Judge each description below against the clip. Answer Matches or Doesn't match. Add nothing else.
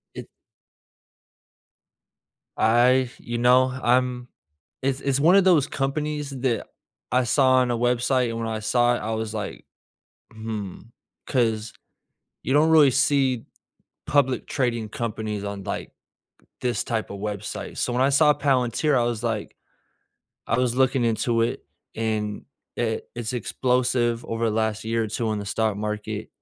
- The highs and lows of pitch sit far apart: Doesn't match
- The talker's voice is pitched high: Doesn't match